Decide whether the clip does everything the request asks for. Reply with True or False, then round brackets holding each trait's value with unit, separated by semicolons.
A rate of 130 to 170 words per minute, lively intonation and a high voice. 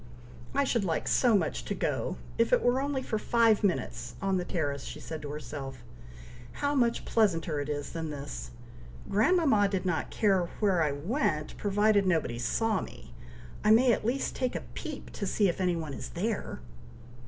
False (185 wpm; 6.7 semitones; 195 Hz)